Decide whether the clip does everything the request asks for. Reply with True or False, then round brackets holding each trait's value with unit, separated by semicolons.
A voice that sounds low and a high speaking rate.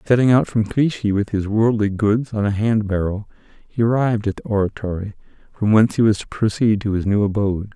True (105 Hz; 210 wpm)